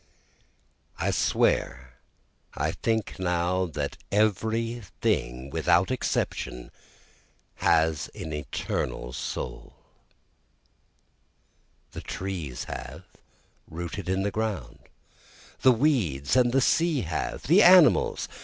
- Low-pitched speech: Yes, very low, 95 Hz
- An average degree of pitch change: No, wide, 7.0 semitones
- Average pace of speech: No, slow, 100 wpm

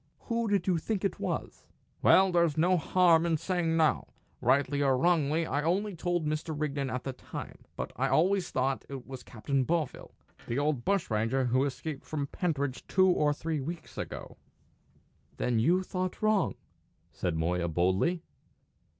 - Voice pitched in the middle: Yes, medium, 155 Hz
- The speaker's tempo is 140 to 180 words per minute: Yes, average, 160 wpm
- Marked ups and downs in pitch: No, average, 4.9 semitones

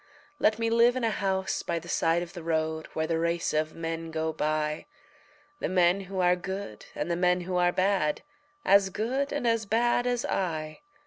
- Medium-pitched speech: Yes, medium, 180 Hz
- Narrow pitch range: No, average, 3.9 semitones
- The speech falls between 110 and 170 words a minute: No, average, 200 wpm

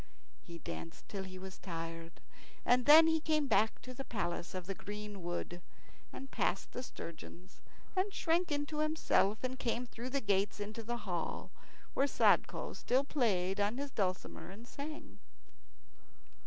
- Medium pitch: No, high, 220 Hz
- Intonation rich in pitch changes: Yes, wide, 7.0 semitones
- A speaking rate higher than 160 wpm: No, average, 155 wpm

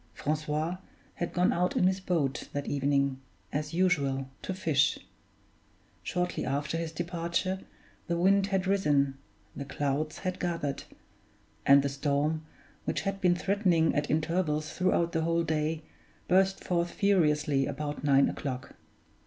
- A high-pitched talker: No, medium, 160 Hz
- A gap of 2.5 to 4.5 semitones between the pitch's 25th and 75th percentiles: Yes, average, 3.9 semitones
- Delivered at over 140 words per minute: No, slow, 135 wpm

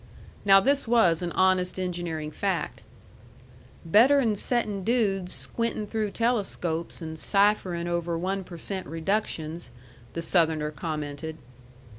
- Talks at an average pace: No, slow, 115 wpm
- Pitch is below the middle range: No, medium, 185 Hz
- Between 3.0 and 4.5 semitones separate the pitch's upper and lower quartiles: Yes, average, 4.1 semitones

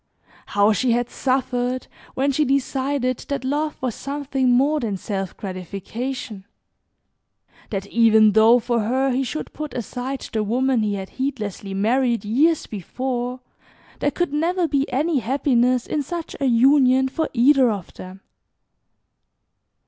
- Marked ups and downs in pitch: No, average, 3.8 semitones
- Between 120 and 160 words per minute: Yes, average, 140 wpm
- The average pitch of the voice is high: Yes, very high, 255 Hz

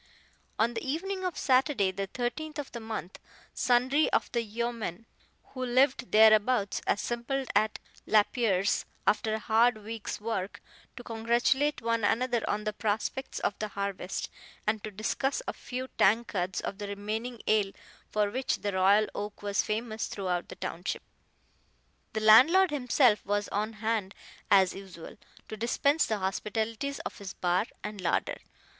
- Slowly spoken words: No, average, 150 wpm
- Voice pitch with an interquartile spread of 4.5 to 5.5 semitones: No, average, 3.2 semitones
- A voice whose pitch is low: No, high, 220 Hz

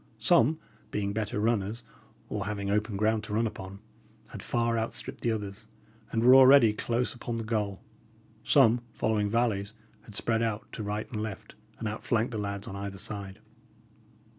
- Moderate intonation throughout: No, narrow, 2.2 semitones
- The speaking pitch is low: Yes, low, 110 Hz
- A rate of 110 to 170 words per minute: Yes, average, 165 wpm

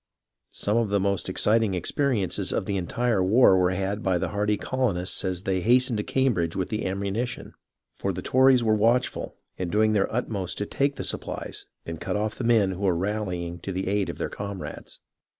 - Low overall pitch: Yes, low, 100 Hz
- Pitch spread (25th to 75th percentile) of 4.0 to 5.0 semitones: No, average, 3.5 semitones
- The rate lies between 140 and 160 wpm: No, average, 200 wpm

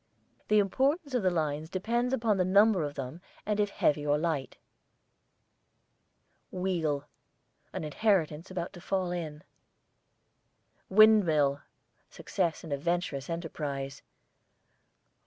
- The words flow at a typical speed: No, slow, 115 wpm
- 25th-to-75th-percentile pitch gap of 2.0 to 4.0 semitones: No, average, 5.2 semitones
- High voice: No, medium, 175 Hz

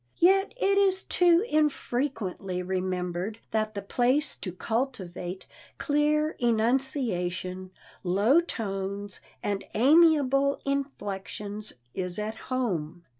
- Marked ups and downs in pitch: Yes, wide, 6.9 semitones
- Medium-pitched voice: No, high, 220 Hz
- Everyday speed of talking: No, slow, 95 wpm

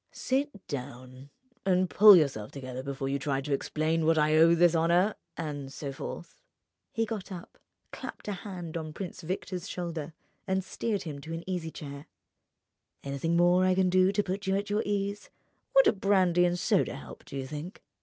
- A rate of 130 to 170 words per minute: No, average, 185 wpm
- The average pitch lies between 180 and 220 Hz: No, medium, 170 Hz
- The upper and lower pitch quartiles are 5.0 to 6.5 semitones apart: No, average, 4.5 semitones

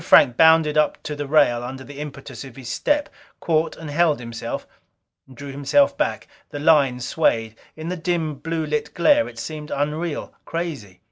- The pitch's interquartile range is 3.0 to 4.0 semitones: Yes, average, 3.4 semitones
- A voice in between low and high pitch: Yes, medium, 150 Hz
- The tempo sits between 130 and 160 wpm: No, average, 175 wpm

